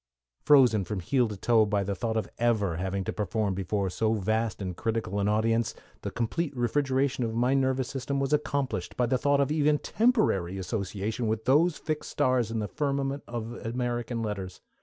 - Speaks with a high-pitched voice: No, low, 115 Hz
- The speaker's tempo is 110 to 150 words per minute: No, average, 180 wpm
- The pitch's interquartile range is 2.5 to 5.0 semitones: Yes, average, 4.5 semitones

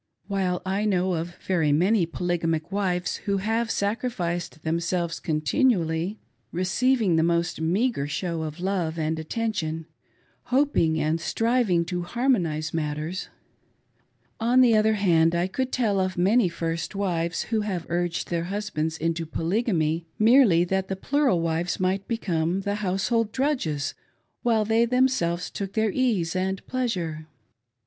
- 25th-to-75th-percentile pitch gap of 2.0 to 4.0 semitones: No, average, 4.6 semitones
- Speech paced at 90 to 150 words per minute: Yes, average, 140 wpm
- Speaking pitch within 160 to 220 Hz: Yes, medium, 185 Hz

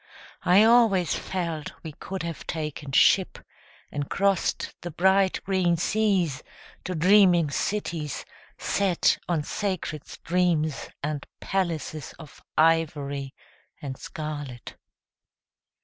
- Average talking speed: No, slow, 100 wpm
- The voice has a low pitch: No, medium, 170 Hz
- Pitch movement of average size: Yes, average, 3.9 semitones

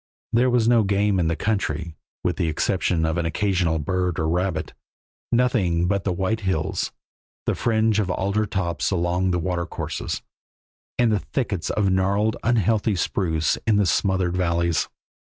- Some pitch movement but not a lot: Yes, average, 3.5 semitones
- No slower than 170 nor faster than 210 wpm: No, average, 155 wpm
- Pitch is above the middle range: No, very low, 95 Hz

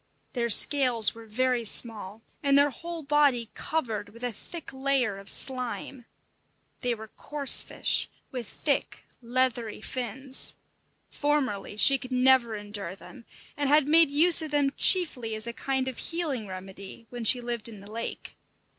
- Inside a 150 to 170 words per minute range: Yes, average, 155 wpm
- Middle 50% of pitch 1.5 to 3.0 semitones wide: No, average, 3.9 semitones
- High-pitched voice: Yes, very high, 250 Hz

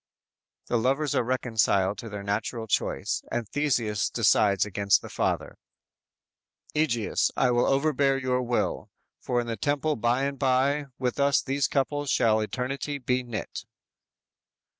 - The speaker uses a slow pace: No, average, 145 wpm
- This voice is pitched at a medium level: No, low, 125 Hz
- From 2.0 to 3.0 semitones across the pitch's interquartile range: No, average, 3.7 semitones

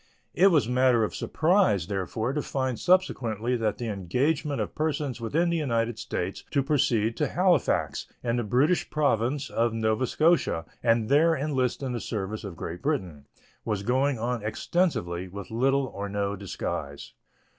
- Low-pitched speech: Yes, low, 120 Hz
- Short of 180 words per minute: Yes, average, 160 wpm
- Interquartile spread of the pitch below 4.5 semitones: No, average, 5.2 semitones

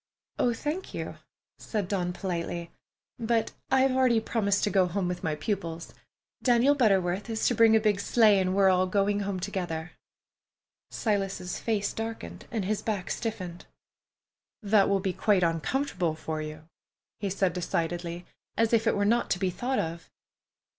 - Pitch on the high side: Yes, high, 200 Hz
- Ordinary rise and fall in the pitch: Yes, average, 3.9 semitones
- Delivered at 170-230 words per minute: No, average, 160 wpm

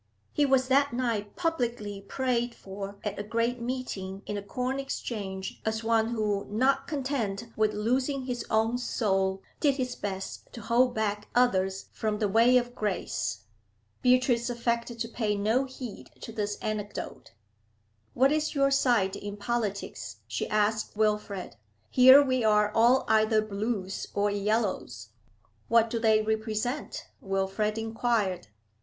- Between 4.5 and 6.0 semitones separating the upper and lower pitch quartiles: No, average, 3.2 semitones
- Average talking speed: Yes, average, 145 wpm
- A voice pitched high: Yes, high, 220 Hz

